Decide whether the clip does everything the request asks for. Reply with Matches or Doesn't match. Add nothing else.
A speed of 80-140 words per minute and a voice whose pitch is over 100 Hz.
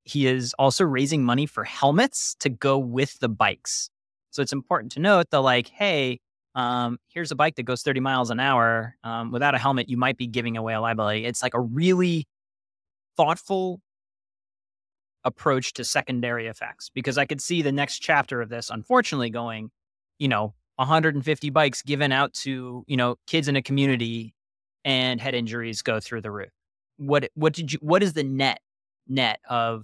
Doesn't match